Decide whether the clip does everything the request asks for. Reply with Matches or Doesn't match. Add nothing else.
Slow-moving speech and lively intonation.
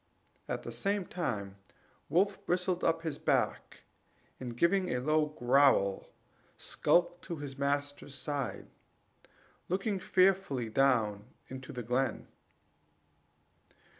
Matches